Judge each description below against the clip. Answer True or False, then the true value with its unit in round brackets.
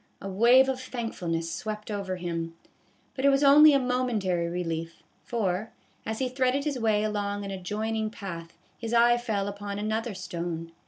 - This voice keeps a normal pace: True (165 wpm)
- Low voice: False (210 Hz)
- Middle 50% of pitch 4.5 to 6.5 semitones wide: True (4.8 semitones)